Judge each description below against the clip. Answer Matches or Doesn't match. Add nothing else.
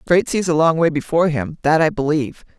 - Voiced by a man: Doesn't match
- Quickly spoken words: Matches